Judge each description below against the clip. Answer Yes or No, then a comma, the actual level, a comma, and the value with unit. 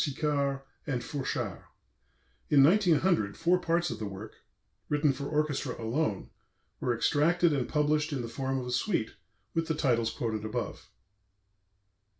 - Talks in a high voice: No, medium, 140 Hz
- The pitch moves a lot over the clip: No, average, 4.6 semitones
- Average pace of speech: Yes, average, 145 wpm